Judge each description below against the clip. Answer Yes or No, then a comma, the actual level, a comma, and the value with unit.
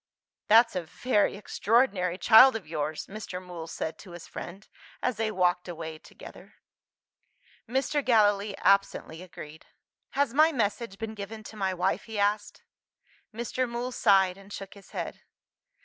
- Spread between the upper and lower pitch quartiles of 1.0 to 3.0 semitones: No, average, 3.9 semitones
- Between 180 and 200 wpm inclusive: No, average, 150 wpm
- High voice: Yes, high, 200 Hz